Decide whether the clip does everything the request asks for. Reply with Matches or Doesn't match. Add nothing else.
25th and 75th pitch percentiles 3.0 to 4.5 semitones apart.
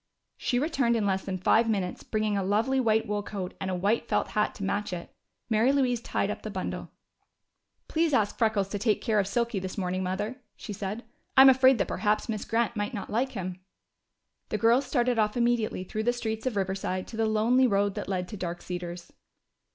Matches